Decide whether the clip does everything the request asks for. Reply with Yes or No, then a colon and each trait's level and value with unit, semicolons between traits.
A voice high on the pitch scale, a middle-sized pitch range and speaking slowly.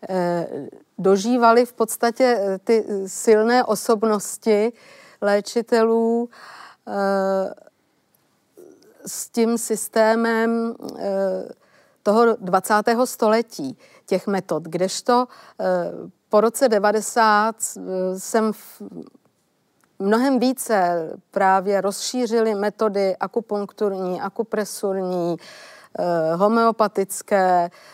Yes: high, 215 Hz; average, 3.1 semitones; slow, 60 wpm